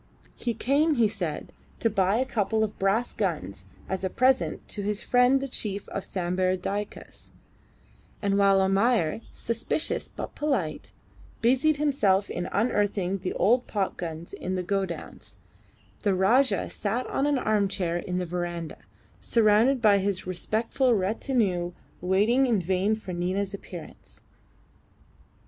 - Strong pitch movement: No, average, 4.1 semitones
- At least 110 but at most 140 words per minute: Yes, slow, 135 wpm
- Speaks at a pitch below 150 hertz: No, high, 200 Hz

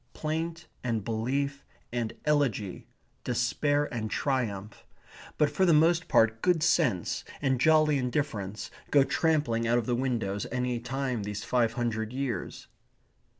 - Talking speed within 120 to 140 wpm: Yes, slow, 135 wpm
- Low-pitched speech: Yes, low, 125 Hz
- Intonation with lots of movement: No, average, 4.5 semitones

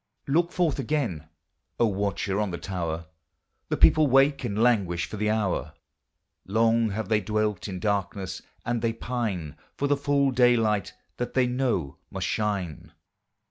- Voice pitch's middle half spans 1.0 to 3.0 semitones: No, average, 4.2 semitones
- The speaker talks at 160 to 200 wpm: No, average, 150 wpm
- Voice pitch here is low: Yes, low, 110 Hz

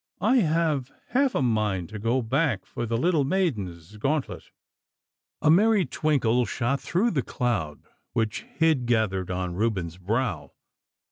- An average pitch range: No, wide, 7.0 semitones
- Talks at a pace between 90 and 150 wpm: Yes, average, 140 wpm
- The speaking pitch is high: No, low, 120 Hz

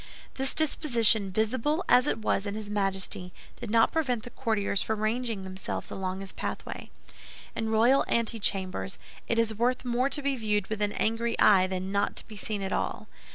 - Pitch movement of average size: Yes, average, 3.1 semitones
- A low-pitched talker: No, high, 220 Hz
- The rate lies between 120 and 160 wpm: No, average, 185 wpm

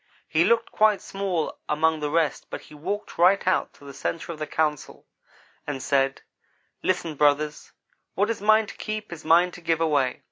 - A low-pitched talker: No, medium, 165 Hz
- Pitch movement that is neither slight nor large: Yes, average, 4.5 semitones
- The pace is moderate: Yes, average, 185 wpm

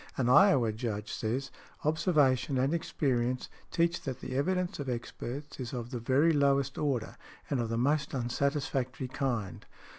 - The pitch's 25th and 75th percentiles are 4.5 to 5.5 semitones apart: No, average, 3.2 semitones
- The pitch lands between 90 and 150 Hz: Yes, low, 135 Hz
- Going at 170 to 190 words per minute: No, average, 150 wpm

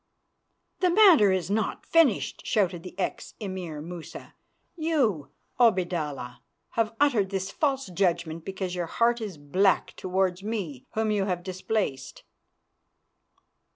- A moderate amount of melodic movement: Yes, average, 4.1 semitones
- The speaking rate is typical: No, slow, 120 wpm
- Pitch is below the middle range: No, high, 190 Hz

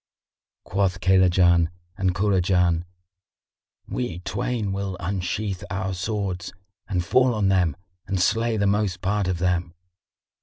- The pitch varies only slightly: Yes, narrow, 2.1 semitones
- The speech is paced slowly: Yes, slow, 120 wpm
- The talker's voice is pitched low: Yes, very low, 95 Hz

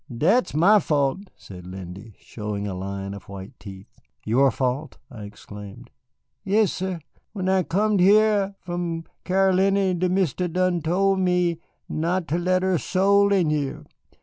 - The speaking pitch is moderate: Yes, medium, 175 Hz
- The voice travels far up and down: Yes, wide, 8.6 semitones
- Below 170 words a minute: Yes, average, 145 wpm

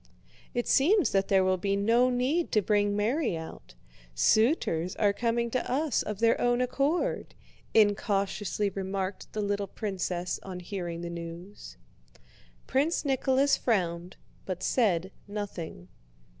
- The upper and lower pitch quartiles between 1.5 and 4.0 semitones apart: No, average, 4.6 semitones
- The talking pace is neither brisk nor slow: No, slow, 130 wpm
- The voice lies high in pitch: Yes, high, 205 Hz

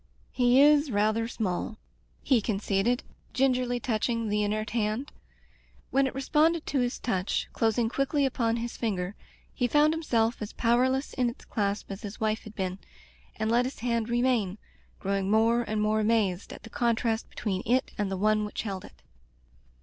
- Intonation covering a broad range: No, average, 2.9 semitones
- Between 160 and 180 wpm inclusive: Yes, average, 175 wpm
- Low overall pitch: No, high, 225 Hz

